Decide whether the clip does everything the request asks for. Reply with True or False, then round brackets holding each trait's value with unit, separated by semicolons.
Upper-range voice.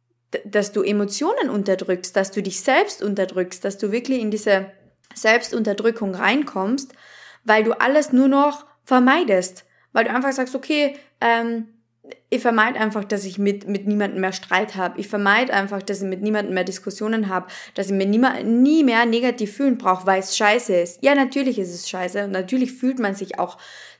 True (210 Hz)